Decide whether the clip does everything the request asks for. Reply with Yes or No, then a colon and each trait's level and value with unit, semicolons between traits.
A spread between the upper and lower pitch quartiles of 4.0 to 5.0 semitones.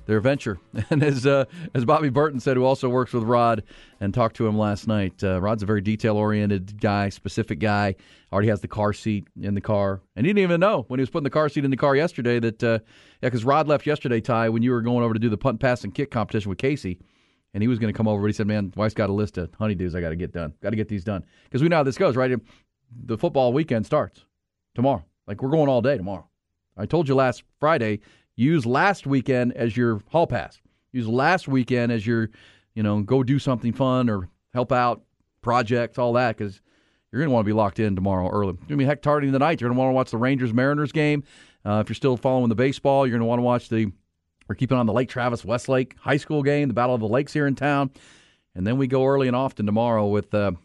Yes: average, 4.3 semitones